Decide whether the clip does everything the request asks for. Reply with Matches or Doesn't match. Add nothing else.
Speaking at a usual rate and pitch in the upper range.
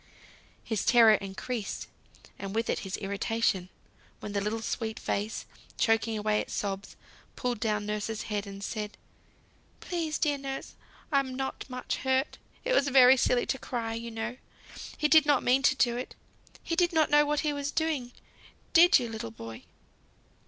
Matches